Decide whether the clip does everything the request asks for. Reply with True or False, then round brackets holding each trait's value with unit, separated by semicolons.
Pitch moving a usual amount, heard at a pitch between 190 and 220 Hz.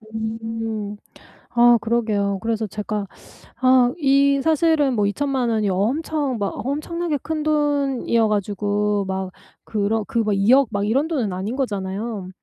False (5.0 semitones; 230 Hz)